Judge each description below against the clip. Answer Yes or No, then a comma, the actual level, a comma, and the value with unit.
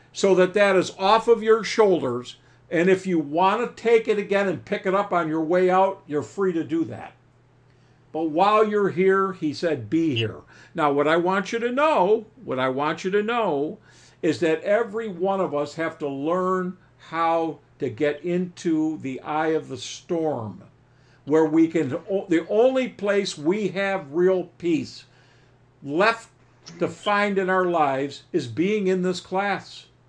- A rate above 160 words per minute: Yes, average, 180 wpm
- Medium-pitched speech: Yes, medium, 170 Hz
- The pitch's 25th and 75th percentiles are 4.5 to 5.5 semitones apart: Yes, average, 5.2 semitones